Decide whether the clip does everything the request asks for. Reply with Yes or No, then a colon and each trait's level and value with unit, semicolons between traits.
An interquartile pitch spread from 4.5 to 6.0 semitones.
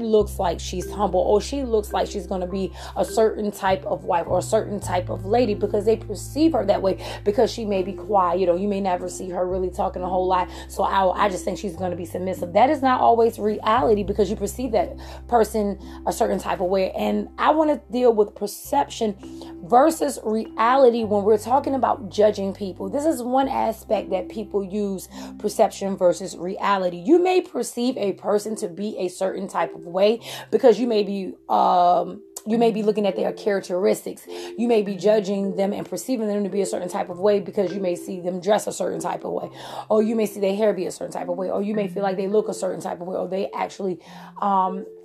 No: average, 2.8 semitones